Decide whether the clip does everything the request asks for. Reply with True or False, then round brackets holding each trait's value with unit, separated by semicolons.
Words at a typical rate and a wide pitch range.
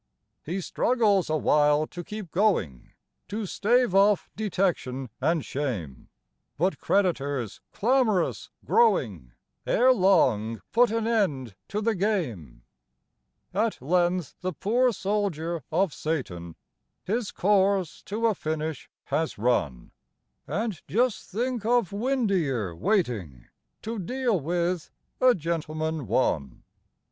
False (110 wpm; 7.0 semitones)